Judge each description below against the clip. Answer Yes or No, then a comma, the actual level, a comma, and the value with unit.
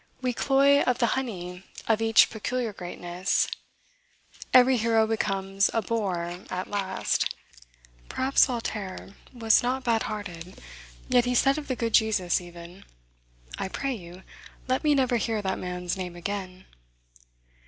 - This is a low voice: No, high, 215 Hz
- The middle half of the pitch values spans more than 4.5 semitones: Yes, average, 5.1 semitones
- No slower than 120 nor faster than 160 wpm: Yes, average, 140 wpm